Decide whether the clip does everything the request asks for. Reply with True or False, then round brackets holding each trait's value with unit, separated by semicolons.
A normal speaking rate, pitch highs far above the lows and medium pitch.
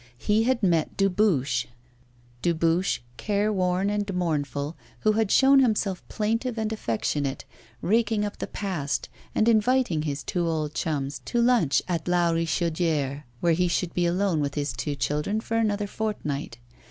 True (150 wpm; 5.9 semitones; 180 Hz)